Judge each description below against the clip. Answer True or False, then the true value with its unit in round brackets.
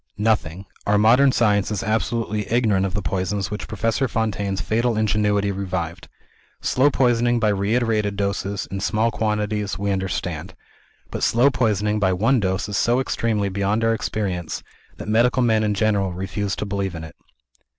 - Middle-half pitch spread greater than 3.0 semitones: False (2.4 semitones)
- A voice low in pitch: True (105 Hz)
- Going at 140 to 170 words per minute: True (160 wpm)